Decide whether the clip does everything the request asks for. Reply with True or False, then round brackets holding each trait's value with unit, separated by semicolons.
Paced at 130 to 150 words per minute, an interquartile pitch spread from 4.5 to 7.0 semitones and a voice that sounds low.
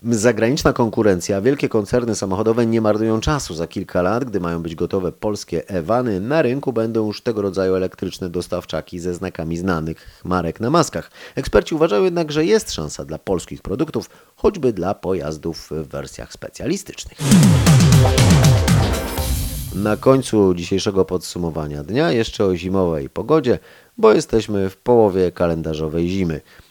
True (135 wpm; 4.9 semitones; 95 Hz)